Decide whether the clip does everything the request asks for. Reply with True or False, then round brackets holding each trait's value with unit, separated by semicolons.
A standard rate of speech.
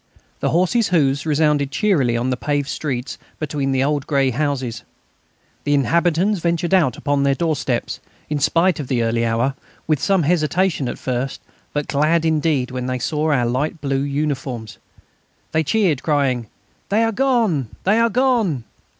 True (160 wpm)